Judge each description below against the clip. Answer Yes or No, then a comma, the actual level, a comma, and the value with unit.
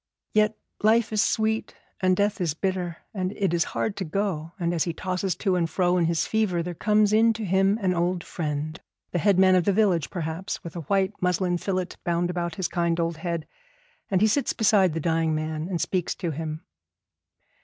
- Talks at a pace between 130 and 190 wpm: No, fast, 205 wpm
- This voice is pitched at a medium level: Yes, medium, 180 Hz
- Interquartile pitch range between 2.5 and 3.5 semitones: Yes, average, 2.9 semitones